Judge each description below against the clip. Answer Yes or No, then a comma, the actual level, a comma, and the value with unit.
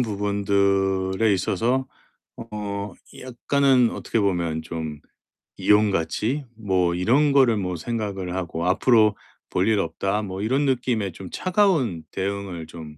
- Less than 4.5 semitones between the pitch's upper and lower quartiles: Yes, average, 4.1 semitones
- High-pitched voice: No, low, 100 Hz